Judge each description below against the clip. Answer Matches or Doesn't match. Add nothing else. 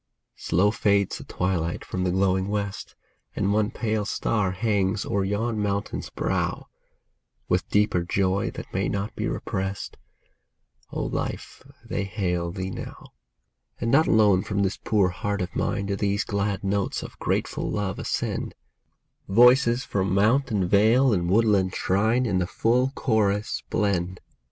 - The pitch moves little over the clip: Matches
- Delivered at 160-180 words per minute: Doesn't match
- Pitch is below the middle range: Matches